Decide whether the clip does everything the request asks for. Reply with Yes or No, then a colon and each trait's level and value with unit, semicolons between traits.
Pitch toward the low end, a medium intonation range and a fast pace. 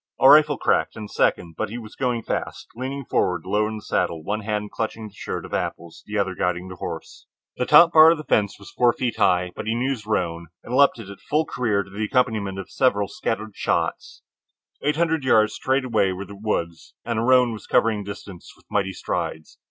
Yes: low, 110 Hz; average, 4.2 semitones; fast, 230 wpm